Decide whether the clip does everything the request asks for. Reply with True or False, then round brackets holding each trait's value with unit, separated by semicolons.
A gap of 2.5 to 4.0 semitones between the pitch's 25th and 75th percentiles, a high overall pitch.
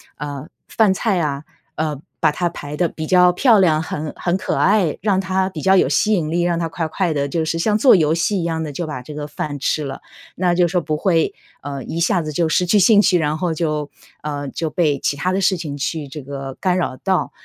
False (3.5 semitones; 165 Hz)